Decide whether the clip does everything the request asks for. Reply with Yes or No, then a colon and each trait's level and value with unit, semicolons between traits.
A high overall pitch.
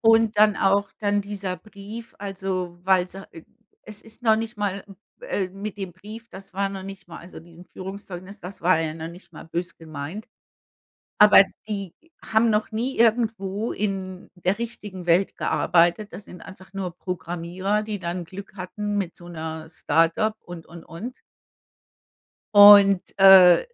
Yes: high, 195 Hz